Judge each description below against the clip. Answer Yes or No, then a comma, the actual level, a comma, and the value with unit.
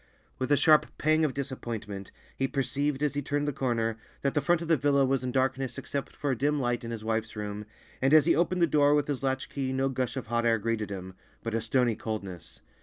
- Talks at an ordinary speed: No, fast, 245 wpm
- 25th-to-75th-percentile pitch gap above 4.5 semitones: No, average, 4.1 semitones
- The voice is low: Yes, low, 130 Hz